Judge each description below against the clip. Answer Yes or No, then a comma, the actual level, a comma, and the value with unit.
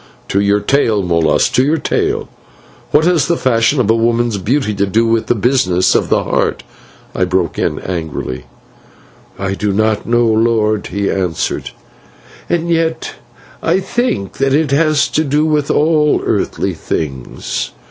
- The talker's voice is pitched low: Yes, low, 115 Hz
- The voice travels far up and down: Yes, wide, 6.9 semitones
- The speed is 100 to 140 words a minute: No, average, 160 wpm